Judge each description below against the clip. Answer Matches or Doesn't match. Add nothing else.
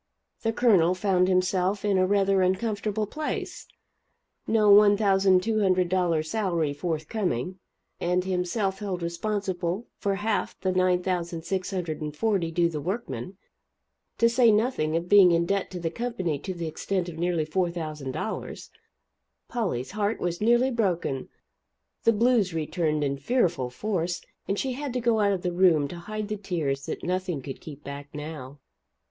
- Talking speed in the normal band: Matches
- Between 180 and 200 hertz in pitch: Matches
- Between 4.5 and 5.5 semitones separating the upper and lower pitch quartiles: Doesn't match